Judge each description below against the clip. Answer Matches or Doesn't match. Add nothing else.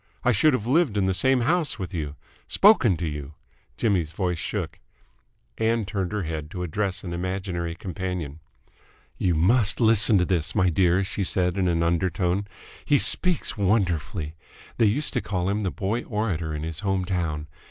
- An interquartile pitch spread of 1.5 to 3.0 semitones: Doesn't match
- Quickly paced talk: Doesn't match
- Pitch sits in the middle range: Doesn't match